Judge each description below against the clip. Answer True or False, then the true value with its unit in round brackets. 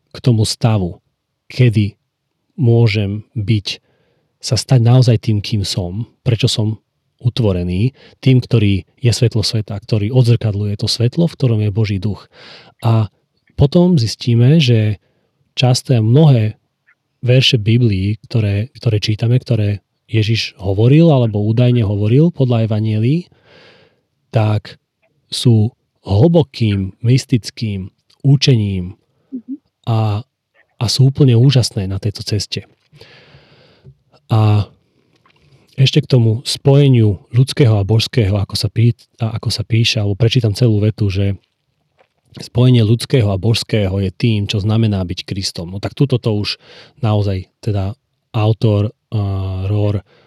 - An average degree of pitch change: True (3.8 semitones)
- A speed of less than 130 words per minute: True (120 wpm)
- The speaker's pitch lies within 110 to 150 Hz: True (115 Hz)